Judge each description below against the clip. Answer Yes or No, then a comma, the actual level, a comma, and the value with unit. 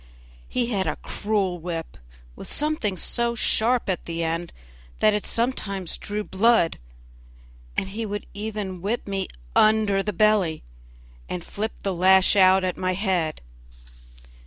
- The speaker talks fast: No, average, 140 wpm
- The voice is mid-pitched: No, high, 200 Hz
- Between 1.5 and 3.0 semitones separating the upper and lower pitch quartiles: Yes, average, 2.7 semitones